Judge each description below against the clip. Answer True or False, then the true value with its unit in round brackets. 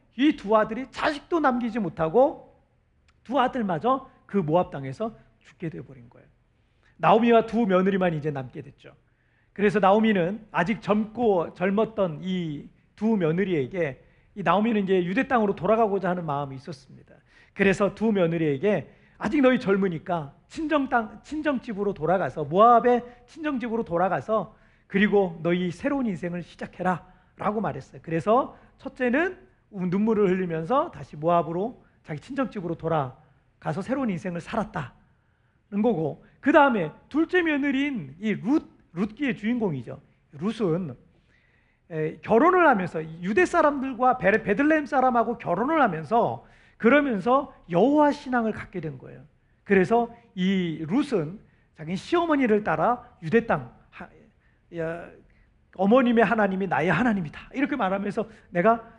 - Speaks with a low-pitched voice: False (205 Hz)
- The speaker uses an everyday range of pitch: False (6.0 semitones)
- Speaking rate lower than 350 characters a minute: True (315 characters per minute)